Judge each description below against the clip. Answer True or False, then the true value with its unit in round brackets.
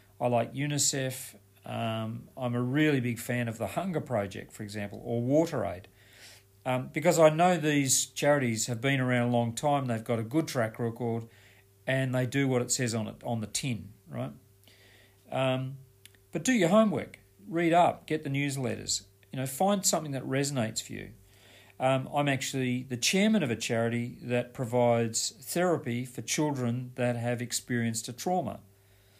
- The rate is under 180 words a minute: True (170 wpm)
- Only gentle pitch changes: False (3.8 semitones)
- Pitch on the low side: True (120 Hz)